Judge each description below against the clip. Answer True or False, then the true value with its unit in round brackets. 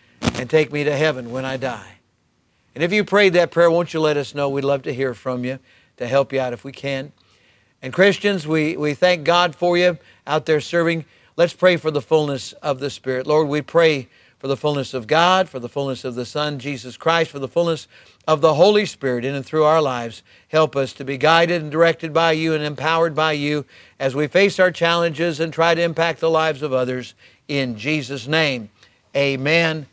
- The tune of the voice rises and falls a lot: False (3.8 semitones)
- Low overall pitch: False (150 Hz)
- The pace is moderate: False (220 wpm)